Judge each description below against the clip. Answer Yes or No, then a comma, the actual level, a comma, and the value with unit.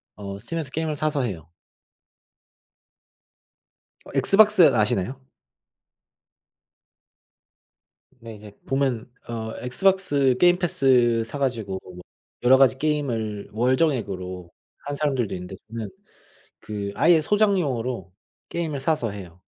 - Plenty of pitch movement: Yes, wide, 6.2 semitones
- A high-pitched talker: No, low, 125 Hz